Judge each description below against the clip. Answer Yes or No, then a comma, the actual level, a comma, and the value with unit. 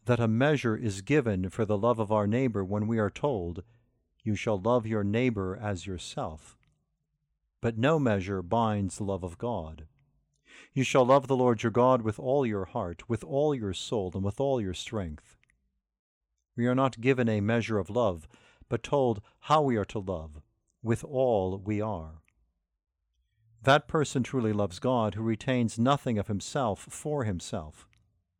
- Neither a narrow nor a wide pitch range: Yes, average, 4.8 semitones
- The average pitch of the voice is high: No, low, 110 Hz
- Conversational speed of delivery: Yes, average, 170 wpm